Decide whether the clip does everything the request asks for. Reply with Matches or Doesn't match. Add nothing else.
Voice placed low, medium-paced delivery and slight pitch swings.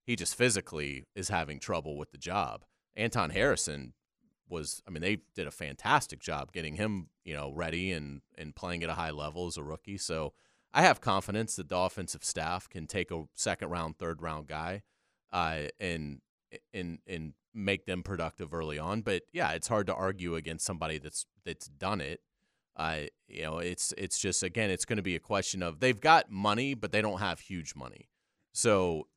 Doesn't match